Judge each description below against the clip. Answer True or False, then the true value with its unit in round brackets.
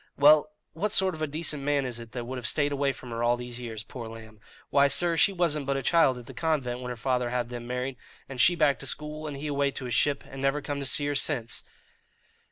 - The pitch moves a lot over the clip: False (3.3 semitones)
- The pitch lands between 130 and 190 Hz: True (135 Hz)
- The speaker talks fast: True (265 wpm)